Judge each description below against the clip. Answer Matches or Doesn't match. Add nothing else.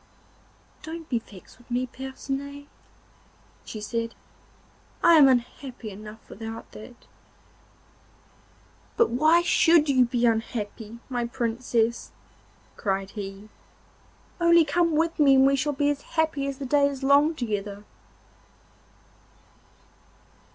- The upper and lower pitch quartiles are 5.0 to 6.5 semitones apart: Doesn't match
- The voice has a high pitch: Matches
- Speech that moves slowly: Matches